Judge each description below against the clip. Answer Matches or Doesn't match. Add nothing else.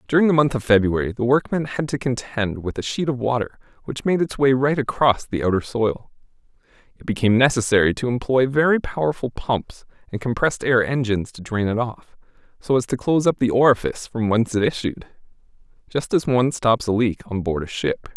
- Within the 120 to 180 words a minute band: Doesn't match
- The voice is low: Matches